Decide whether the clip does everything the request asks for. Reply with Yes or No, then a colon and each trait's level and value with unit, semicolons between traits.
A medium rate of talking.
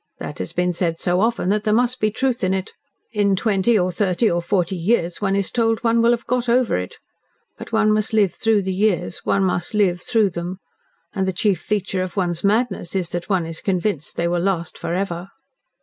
No: fast, 220 wpm